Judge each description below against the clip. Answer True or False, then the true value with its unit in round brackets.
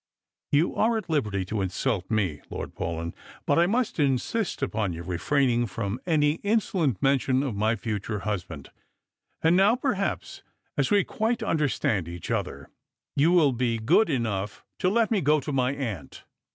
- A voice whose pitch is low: True (130 Hz)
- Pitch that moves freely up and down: True (8.7 semitones)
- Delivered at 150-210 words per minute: True (165 wpm)